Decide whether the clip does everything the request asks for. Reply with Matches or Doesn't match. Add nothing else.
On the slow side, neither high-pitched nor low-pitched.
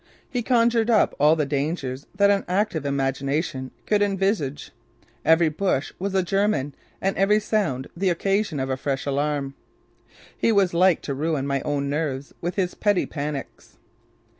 Doesn't match